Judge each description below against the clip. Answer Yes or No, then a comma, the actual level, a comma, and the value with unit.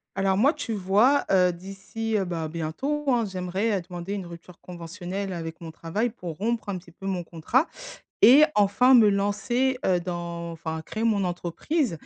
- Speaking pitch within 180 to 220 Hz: Yes, high, 190 Hz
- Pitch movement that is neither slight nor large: Yes, average, 4.4 semitones